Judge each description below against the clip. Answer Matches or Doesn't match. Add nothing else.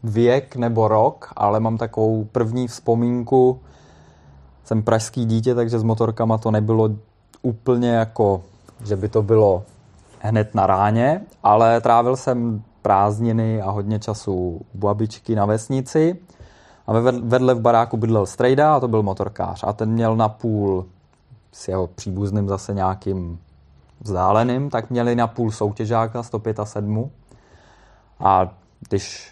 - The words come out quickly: Doesn't match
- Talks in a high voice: Doesn't match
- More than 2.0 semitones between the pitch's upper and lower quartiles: Matches